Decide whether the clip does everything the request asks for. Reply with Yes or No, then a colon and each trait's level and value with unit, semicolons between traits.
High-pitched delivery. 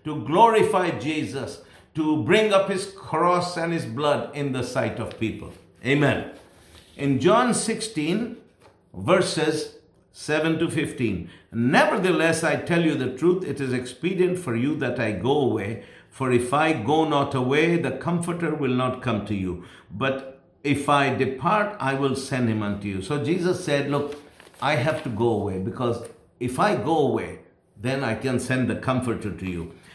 No: medium, 140 Hz